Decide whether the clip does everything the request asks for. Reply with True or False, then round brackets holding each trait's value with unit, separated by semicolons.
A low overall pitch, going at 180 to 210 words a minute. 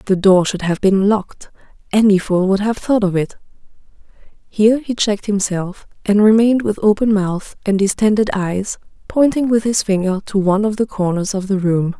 False (200 Hz; 185 wpm)